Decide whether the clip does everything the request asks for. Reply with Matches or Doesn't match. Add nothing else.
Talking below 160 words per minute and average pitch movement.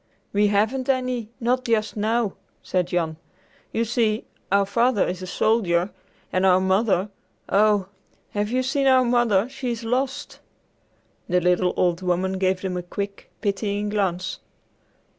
Matches